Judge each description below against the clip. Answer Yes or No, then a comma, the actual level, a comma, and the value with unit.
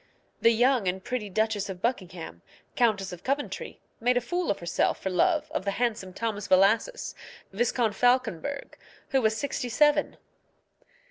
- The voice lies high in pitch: Yes, high, 225 Hz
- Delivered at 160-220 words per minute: No, average, 150 wpm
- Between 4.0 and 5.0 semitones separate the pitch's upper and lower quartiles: Yes, average, 4.5 semitones